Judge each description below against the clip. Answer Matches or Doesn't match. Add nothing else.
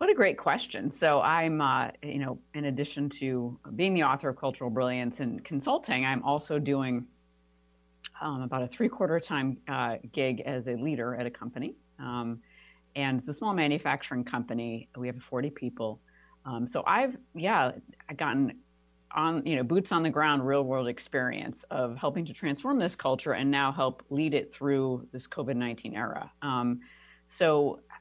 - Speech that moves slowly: Doesn't match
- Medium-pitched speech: Doesn't match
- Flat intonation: Doesn't match